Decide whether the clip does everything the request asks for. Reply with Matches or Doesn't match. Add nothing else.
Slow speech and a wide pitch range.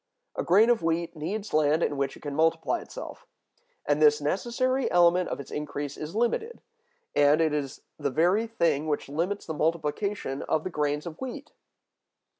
Doesn't match